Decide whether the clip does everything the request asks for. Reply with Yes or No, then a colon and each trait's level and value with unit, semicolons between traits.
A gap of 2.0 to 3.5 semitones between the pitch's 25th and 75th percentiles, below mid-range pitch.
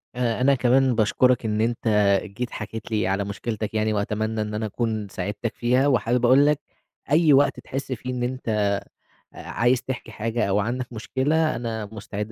Yes: average, 2.9 semitones; low, 115 Hz